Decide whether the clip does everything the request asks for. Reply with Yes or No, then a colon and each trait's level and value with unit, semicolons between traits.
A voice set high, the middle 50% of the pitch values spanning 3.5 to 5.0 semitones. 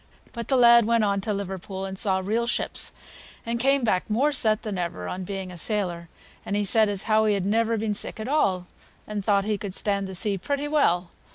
No: high, 205 Hz; average, 3.1 semitones